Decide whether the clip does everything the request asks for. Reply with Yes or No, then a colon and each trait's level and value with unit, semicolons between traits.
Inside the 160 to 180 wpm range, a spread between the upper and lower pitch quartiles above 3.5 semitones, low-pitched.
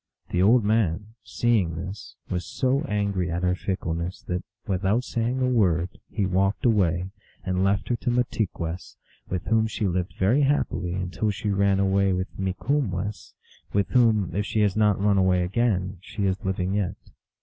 No: average, 170 wpm; average, 3.0 semitones; low, 100 Hz